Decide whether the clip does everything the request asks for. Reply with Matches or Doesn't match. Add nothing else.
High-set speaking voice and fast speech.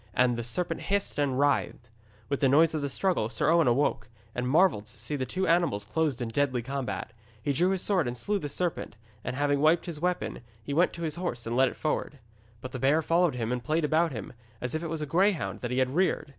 Doesn't match